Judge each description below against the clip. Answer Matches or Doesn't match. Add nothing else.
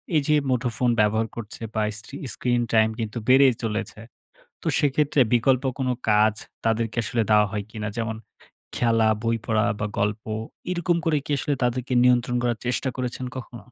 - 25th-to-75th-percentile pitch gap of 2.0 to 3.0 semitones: Matches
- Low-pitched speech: Matches